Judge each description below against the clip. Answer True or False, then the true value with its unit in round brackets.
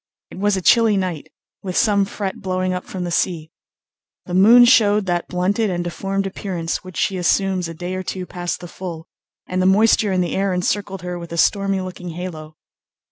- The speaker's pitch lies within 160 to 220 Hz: True (185 Hz)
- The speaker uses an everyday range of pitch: False (1.8 semitones)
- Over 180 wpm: True (200 wpm)